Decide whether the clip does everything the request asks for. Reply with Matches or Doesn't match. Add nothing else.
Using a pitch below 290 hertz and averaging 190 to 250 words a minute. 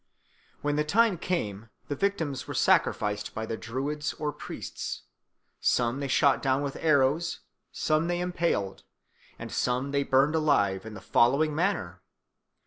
Doesn't match